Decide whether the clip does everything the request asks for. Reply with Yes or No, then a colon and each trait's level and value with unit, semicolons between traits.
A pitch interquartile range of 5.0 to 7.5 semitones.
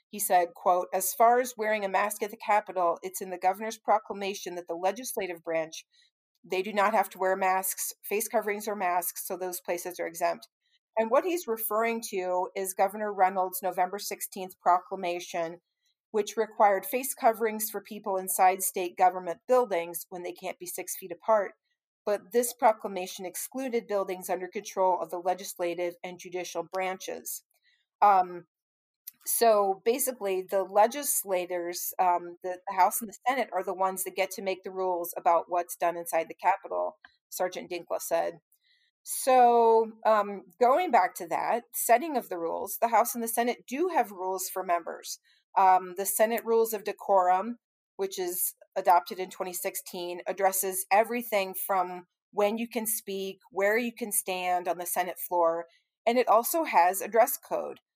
No: average, 3.6 semitones